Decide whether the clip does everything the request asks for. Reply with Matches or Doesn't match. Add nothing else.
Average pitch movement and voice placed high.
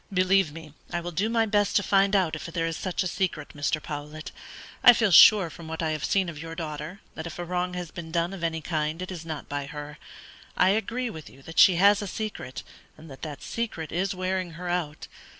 Doesn't match